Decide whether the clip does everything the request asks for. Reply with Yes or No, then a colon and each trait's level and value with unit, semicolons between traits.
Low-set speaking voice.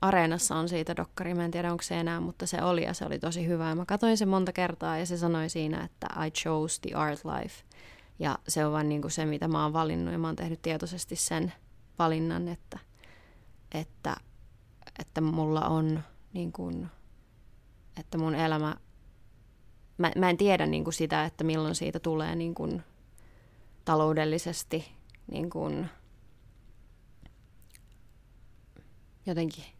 No: medium, 155 Hz